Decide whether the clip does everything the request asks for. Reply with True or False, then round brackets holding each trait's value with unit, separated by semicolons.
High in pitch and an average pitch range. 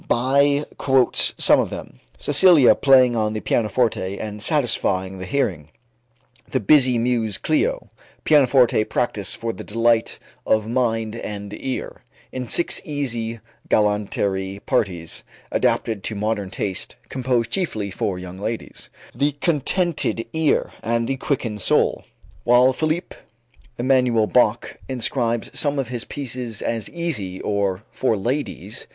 False (115 Hz; 4.2 semitones)